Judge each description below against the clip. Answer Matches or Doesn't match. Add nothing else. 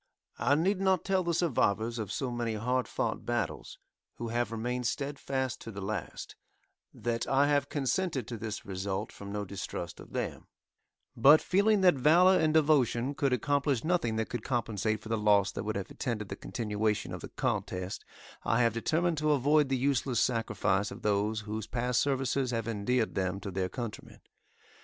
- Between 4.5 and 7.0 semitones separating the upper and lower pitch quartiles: Matches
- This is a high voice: Doesn't match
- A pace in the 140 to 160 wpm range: Doesn't match